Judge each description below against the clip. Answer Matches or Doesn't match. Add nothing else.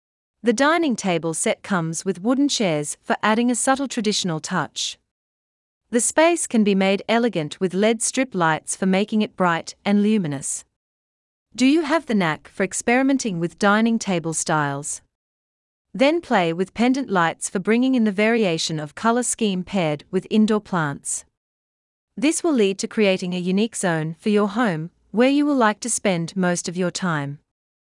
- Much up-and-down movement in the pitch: Matches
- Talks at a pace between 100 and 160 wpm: Doesn't match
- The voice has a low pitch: Doesn't match